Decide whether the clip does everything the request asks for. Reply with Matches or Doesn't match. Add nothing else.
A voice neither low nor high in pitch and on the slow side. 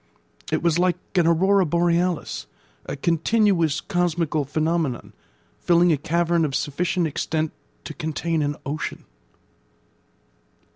Matches